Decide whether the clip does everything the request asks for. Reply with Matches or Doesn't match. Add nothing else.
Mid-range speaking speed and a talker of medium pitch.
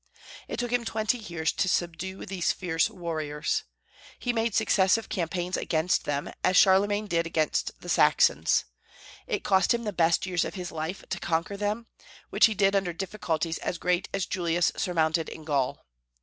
Matches